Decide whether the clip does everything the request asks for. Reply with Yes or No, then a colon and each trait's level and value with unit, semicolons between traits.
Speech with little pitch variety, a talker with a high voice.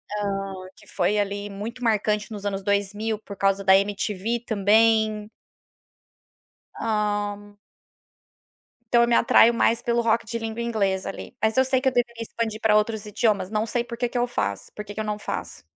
Yes: narrow, 2.2 semitones; high, 215 Hz